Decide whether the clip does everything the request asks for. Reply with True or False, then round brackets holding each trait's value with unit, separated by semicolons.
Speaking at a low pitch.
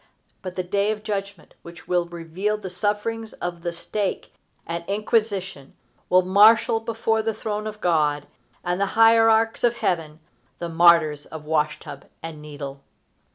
False (185 Hz)